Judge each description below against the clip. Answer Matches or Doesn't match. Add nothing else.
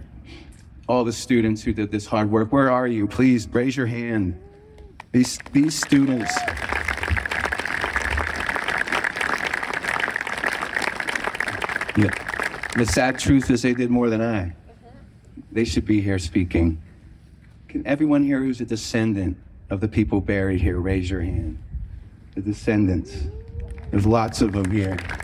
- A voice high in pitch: Doesn't match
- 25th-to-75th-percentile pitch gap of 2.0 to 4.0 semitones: Doesn't match